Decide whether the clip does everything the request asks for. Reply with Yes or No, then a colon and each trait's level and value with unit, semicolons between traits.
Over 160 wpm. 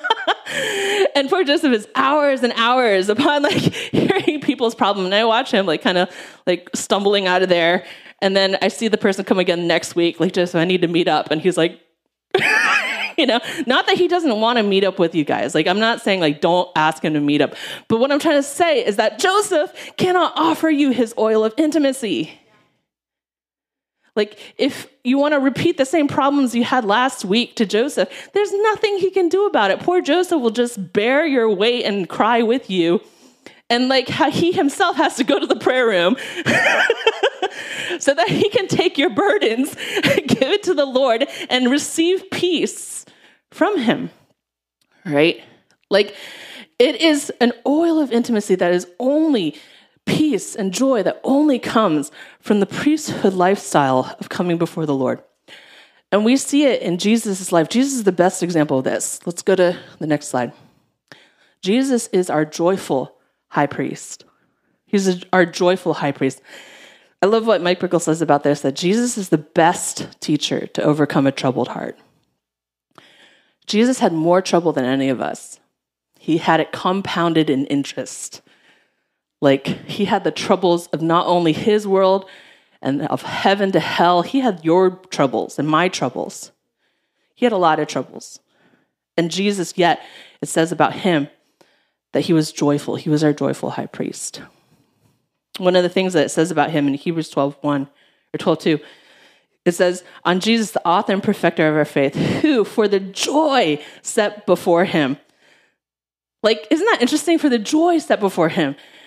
Yes: average, 180 wpm